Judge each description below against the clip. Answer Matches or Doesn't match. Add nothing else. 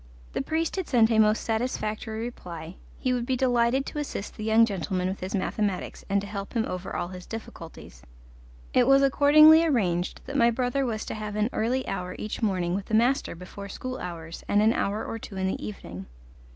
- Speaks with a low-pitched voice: Doesn't match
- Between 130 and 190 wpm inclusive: Doesn't match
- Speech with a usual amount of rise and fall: Matches